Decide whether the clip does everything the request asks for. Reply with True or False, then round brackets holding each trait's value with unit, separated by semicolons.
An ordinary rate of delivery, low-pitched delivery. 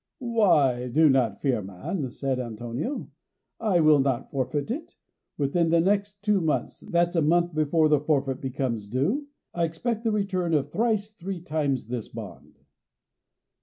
False (155 wpm; 155 Hz)